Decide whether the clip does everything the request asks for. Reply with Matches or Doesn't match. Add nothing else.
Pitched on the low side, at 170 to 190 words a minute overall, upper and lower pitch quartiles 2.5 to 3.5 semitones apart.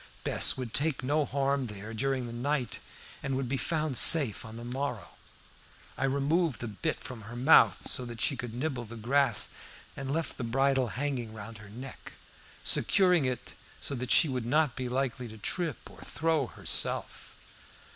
Matches